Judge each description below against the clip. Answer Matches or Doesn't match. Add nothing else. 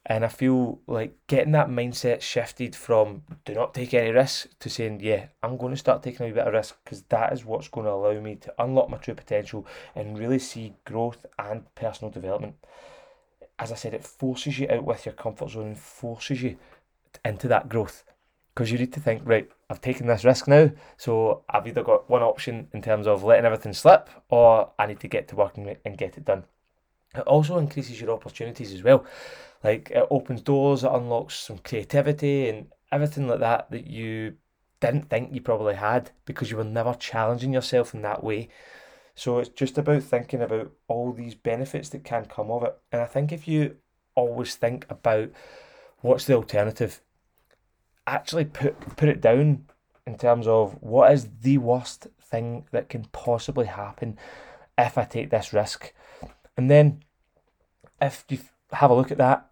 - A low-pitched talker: Matches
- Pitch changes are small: Doesn't match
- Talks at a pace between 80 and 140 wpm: Doesn't match